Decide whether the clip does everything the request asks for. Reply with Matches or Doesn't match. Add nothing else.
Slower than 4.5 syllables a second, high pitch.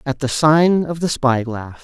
Doesn't match